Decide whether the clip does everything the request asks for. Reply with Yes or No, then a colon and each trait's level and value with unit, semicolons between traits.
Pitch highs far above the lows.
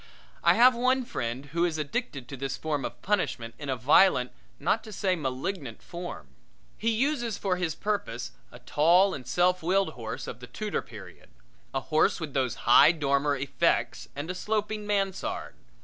Yes: wide, 6.8 semitones